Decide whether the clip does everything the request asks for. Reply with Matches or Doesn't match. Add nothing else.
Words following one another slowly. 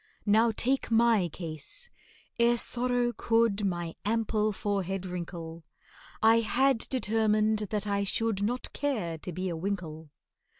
Matches